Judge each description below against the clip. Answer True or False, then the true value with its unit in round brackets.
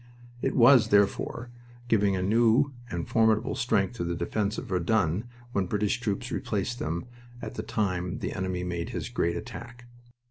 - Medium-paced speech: True (165 wpm)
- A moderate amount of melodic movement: True (4.4 semitones)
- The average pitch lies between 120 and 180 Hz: False (105 Hz)